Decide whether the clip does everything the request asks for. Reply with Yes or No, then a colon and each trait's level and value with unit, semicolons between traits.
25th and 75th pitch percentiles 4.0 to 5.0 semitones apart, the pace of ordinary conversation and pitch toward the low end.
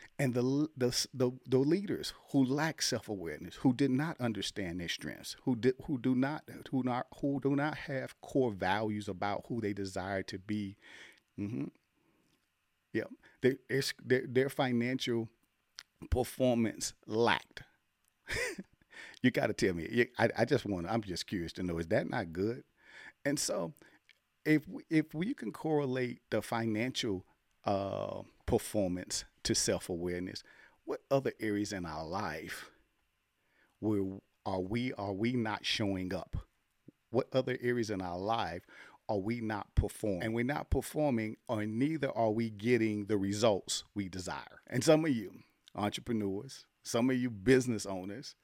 Yes: average, 4.7 semitones; average, 150 wpm; low, 115 Hz